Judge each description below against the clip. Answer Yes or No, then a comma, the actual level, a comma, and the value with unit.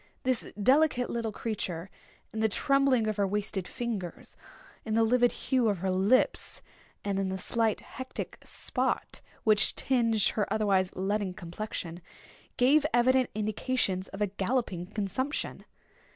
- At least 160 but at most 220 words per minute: No, slow, 135 wpm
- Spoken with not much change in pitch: No, average, 4.1 semitones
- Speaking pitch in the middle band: No, high, 215 Hz